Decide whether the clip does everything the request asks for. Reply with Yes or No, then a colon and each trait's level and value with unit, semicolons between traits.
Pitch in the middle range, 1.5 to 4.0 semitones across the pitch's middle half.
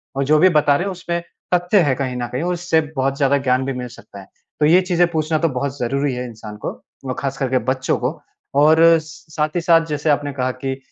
Yes: medium, 145 Hz; average, 3.6 semitones